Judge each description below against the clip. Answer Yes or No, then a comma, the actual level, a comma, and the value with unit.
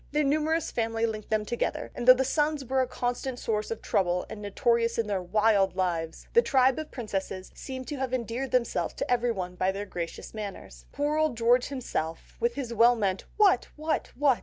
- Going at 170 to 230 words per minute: Yes, average, 200 wpm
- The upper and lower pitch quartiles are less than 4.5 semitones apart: No, average, 4.8 semitones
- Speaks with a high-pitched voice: Yes, high, 235 Hz